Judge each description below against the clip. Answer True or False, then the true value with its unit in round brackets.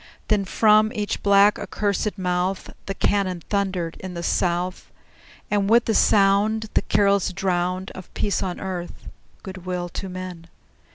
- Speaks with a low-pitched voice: False (190 Hz)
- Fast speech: False (150 wpm)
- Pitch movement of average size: False (2.1 semitones)